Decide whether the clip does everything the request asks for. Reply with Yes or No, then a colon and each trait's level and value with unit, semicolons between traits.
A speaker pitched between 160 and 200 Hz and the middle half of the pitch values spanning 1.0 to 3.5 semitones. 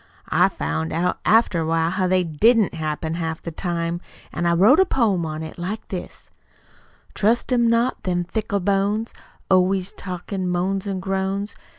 Yes: medium, 185 Hz; average, 3.2 semitones